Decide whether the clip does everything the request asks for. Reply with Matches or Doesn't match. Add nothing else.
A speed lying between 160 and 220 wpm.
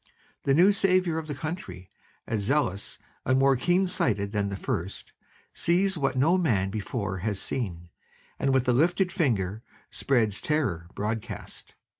Doesn't match